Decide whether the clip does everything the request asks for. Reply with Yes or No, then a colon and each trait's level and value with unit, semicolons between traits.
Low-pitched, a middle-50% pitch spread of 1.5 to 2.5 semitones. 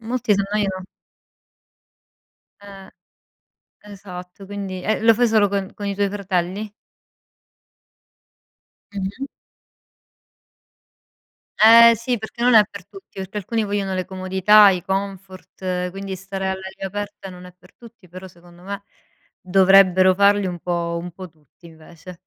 No: high, 195 Hz; narrow, 2.0 semitones